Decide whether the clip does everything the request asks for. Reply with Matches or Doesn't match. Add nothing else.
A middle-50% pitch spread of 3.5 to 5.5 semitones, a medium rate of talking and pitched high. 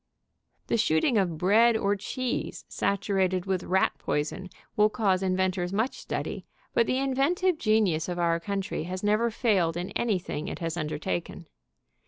Matches